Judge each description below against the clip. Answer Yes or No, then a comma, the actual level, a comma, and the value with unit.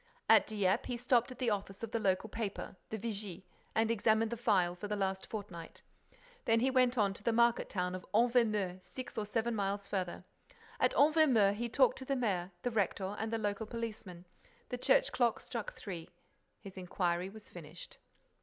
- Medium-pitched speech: No, high, 215 Hz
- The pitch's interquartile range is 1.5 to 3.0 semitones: No, average, 3.5 semitones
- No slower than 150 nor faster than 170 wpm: No, average, 190 wpm